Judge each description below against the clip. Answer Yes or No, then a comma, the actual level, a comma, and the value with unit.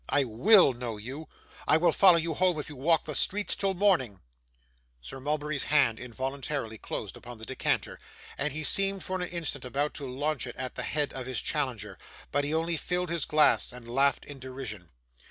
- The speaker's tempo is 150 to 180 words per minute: No, average, 195 wpm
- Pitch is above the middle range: No, medium, 145 Hz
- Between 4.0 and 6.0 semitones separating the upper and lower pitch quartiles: Yes, average, 4.3 semitones